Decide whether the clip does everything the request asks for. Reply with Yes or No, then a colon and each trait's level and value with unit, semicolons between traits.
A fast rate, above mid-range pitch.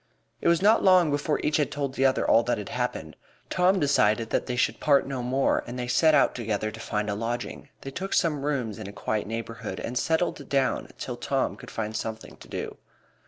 No: fast, 225 wpm; low, 130 Hz